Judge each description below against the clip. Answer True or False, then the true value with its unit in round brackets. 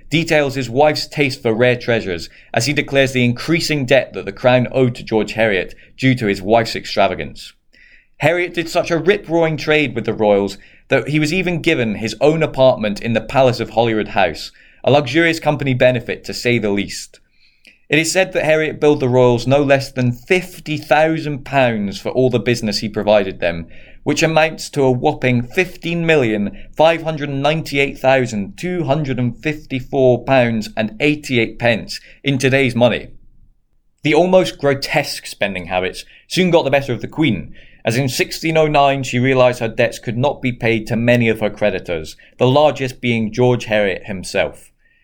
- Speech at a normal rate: True (185 wpm)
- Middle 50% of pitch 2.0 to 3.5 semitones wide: False (4.8 semitones)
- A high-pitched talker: False (130 Hz)